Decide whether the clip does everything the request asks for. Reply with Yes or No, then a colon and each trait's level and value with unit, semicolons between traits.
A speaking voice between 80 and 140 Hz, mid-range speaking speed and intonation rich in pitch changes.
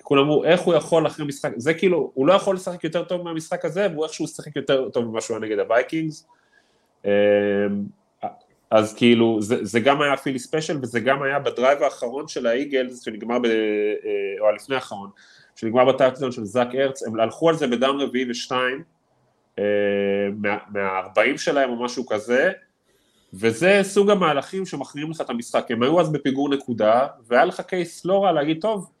No: low, 135 Hz; fast, 175 wpm; wide, 5.8 semitones